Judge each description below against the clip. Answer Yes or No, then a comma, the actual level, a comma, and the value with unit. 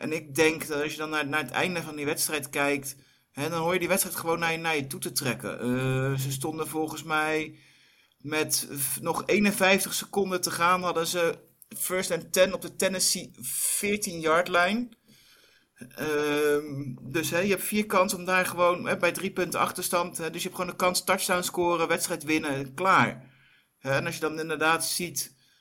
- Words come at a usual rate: Yes, average, 190 wpm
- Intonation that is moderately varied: Yes, average, 3.4 semitones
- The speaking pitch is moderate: Yes, medium, 165 Hz